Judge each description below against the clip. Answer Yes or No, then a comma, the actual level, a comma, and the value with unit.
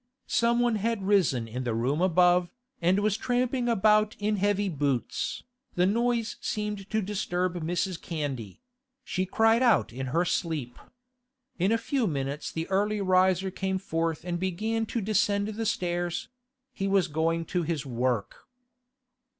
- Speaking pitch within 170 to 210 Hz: Yes, medium, 185 Hz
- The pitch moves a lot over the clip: No, average, 4.5 semitones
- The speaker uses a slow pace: No, average, 150 wpm